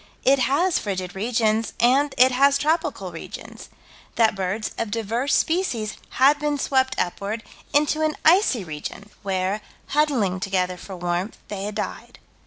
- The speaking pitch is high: Yes, high, 225 Hz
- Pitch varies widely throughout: Yes, wide, 6.1 semitones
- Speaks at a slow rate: No, average, 145 wpm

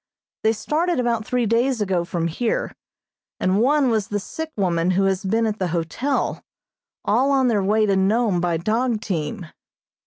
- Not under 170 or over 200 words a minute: Yes, average, 175 wpm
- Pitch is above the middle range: Yes, high, 215 Hz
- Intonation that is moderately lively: Yes, average, 4.3 semitones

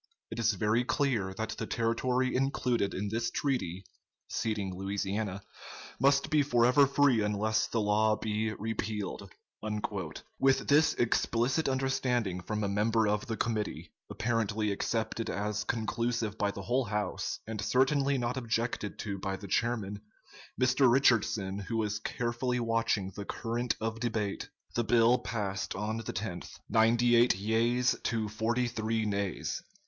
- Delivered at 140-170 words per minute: Yes, average, 145 wpm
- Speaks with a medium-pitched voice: No, low, 115 Hz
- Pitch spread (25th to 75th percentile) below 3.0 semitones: Yes, narrow, 2.6 semitones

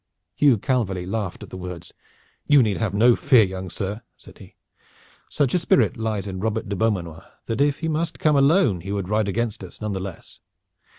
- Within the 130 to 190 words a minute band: No, average, 200 wpm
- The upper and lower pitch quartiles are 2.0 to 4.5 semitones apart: No, average, 5.3 semitones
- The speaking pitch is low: Yes, low, 110 Hz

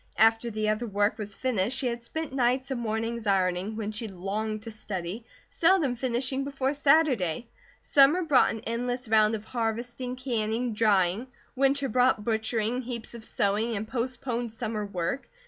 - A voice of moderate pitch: No, high, 230 Hz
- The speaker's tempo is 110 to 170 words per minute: Yes, average, 160 wpm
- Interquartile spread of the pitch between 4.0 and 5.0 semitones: No, average, 3.1 semitones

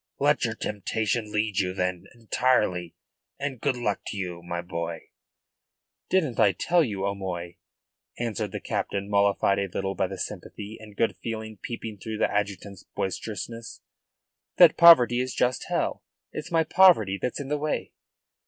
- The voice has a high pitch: No, low, 105 Hz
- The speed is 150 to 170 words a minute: Yes, average, 155 wpm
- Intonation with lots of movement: No, average, 4.1 semitones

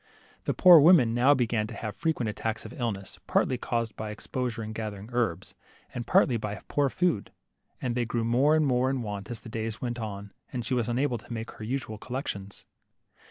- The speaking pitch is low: Yes, low, 120 Hz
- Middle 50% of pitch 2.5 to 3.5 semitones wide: Yes, average, 2.8 semitones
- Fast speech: Yes, fast, 210 wpm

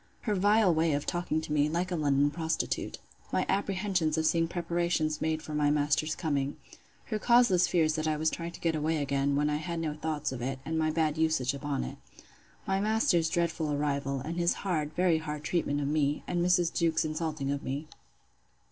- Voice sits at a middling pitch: Yes, medium, 160 Hz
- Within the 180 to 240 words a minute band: Yes, average, 200 wpm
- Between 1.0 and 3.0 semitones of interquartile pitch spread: Yes, narrow, 2.6 semitones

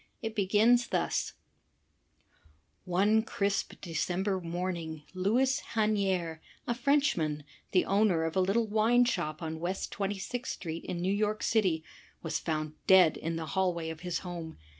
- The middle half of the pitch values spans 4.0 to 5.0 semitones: Yes, average, 4.4 semitones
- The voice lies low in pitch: No, medium, 185 Hz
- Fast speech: No, average, 145 wpm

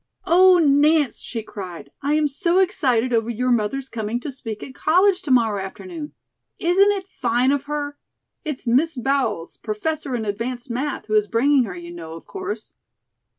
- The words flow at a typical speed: Yes, average, 175 wpm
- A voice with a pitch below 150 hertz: No, very high, 260 Hz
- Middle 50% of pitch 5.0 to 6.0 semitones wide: Yes, wide, 5.4 semitones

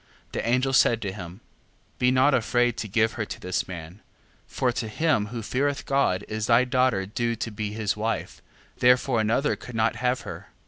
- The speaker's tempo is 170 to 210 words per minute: Yes, average, 190 wpm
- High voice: No, low, 115 Hz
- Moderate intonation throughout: Yes, average, 3.1 semitones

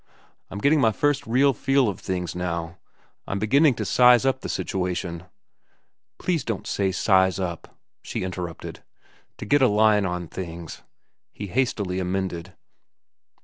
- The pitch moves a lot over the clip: Yes, wide, 5.8 semitones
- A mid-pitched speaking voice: No, very low, 95 Hz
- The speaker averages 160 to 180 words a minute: No, average, 145 wpm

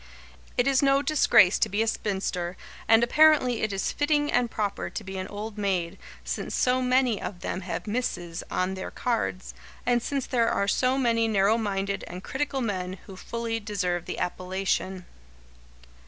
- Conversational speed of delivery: Yes, average, 170 wpm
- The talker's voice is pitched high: Yes, high, 215 Hz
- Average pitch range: Yes, average, 4.7 semitones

